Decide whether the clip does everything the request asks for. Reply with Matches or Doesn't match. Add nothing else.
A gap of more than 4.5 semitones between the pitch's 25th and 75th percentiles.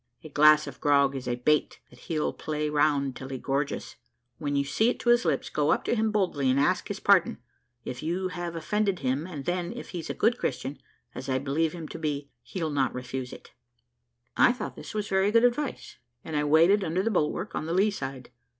Matches